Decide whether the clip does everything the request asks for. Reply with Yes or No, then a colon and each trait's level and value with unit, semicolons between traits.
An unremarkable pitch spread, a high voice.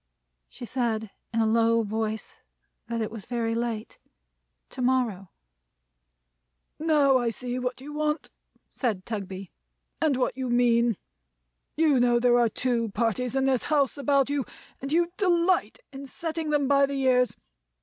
Yes: average, 3.4 semitones; very high, 250 Hz